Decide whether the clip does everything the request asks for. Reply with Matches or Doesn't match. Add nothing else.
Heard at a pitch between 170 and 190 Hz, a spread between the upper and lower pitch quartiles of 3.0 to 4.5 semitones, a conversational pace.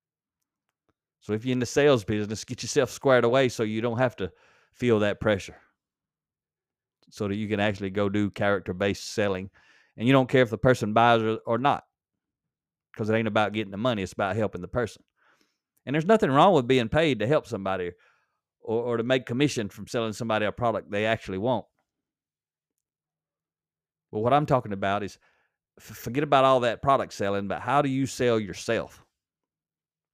Doesn't match